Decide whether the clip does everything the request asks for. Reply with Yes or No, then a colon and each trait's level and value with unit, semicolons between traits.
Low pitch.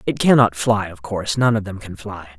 Yes: low, 105 Hz